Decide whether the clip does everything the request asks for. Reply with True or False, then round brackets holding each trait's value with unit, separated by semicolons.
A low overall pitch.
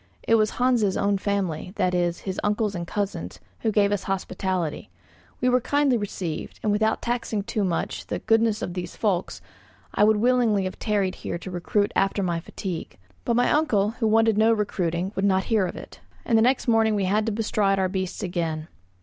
False (205 Hz)